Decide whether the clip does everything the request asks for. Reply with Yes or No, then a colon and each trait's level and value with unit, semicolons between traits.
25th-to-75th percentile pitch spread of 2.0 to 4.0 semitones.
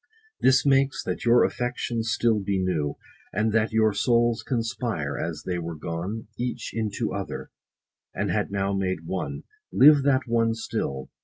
No: average, 4.4 semitones